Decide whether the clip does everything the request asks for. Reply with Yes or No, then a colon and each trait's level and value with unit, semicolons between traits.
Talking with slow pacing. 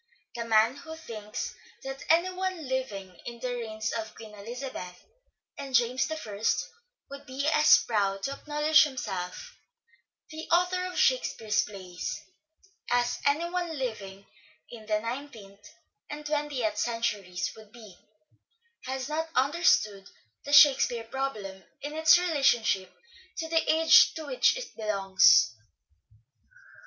Yes: slow, 125 wpm